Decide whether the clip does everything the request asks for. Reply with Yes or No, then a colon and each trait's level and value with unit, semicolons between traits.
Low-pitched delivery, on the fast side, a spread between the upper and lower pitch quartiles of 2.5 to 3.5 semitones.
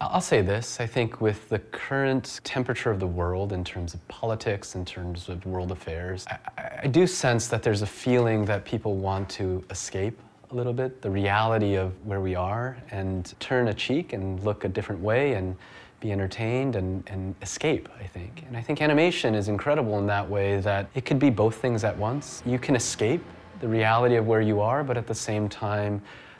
No: low, 105 Hz; fast, 210 wpm; average, 4.0 semitones